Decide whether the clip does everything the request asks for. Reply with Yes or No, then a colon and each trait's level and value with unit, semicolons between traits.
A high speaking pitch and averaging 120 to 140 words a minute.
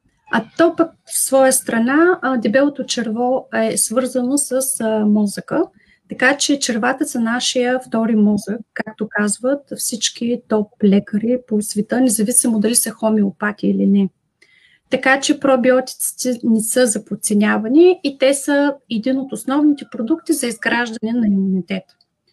Yes: high, 245 Hz; average, 130 wpm